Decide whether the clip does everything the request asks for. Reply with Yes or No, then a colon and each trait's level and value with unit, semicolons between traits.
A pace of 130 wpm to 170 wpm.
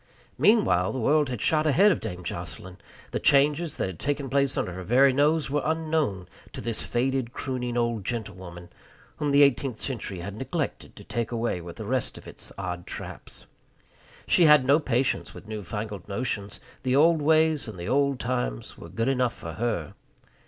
No: average, 180 wpm